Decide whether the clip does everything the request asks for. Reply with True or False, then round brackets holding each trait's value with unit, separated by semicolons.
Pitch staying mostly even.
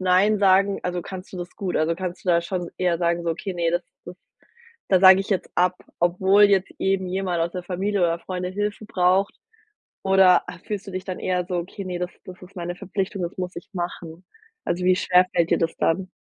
True (1.5 semitones)